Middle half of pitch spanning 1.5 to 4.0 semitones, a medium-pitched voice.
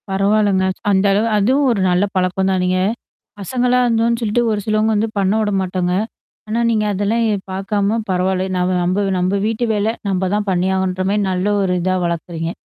No: narrow, 2.6 semitones; high, 195 Hz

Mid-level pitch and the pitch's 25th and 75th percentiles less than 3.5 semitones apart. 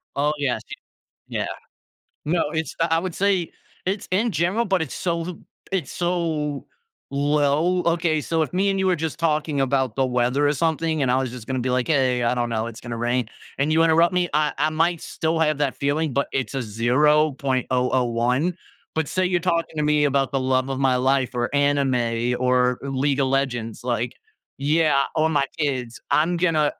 No: medium, 145 Hz; average, 4.2 semitones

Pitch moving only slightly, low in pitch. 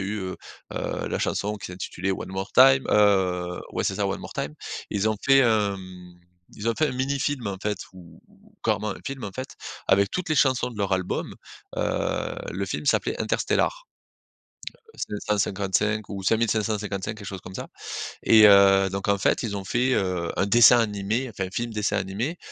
No: average, 3.3 semitones; low, 105 Hz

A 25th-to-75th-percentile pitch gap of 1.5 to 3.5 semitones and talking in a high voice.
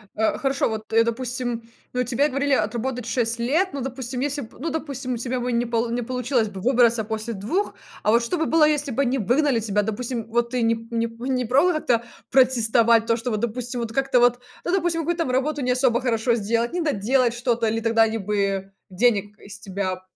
Yes: average, 2.7 semitones; high, 240 Hz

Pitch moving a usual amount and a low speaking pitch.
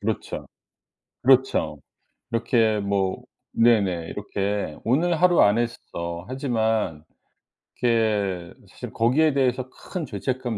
Yes: average, 4.4 semitones; low, 115 Hz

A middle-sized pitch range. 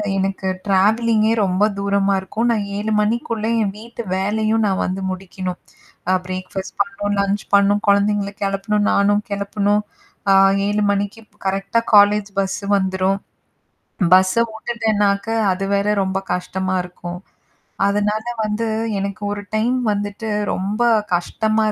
No: narrow, 1.5 semitones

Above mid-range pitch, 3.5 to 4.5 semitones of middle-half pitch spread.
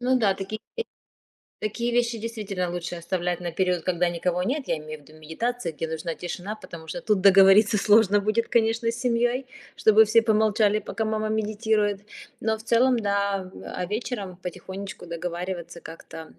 Yes: high, 200 Hz; average, 3.8 semitones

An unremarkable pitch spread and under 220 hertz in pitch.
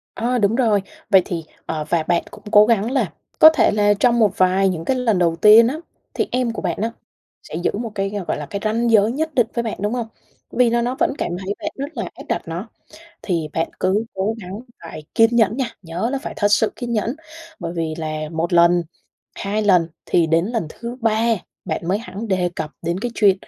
Yes: average, 4.9 semitones; high, 210 Hz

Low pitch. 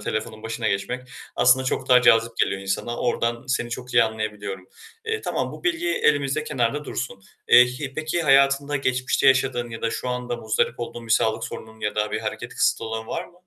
Yes: low, 120 Hz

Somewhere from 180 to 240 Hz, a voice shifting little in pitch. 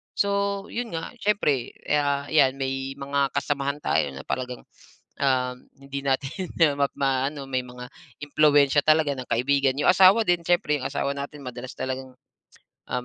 No: medium, 140 Hz; narrow, 2.2 semitones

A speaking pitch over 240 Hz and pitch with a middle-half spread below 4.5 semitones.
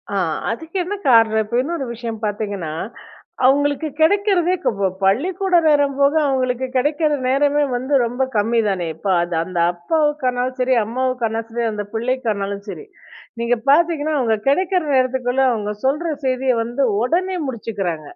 No: very high, 255 Hz; average, 4.9 semitones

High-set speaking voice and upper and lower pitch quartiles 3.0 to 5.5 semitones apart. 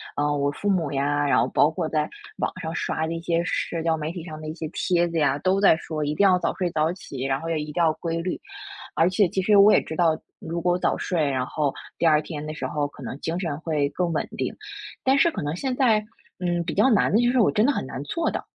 No: medium, 165 Hz; average, 3.3 semitones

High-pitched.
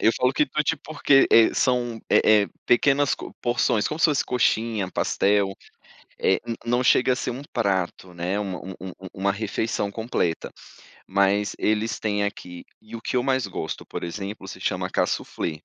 No: low, 110 Hz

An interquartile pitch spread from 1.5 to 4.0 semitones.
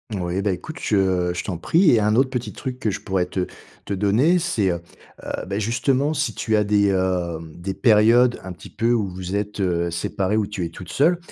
No: average, 4.5 semitones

